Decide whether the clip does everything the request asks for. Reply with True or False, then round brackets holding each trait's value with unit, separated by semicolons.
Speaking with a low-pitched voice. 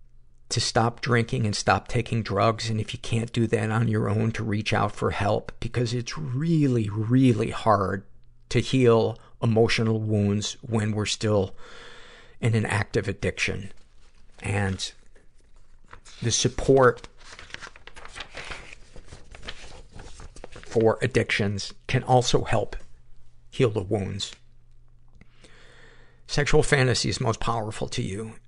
True (110 Hz)